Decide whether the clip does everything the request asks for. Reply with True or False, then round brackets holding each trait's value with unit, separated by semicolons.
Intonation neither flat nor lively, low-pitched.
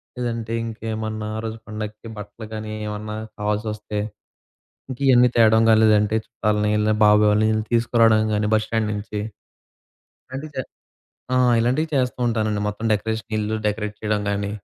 False (1.2 semitones; 110 Hz)